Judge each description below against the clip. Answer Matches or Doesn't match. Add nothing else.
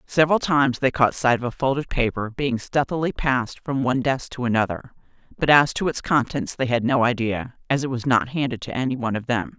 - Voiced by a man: Doesn't match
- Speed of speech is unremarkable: Doesn't match